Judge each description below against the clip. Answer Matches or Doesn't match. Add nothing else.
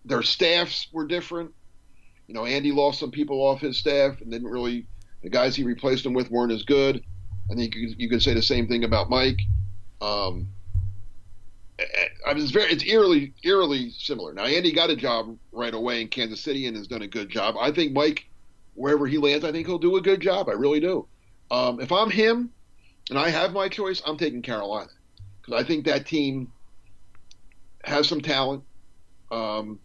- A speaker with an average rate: Matches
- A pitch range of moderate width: Doesn't match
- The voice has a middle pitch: Doesn't match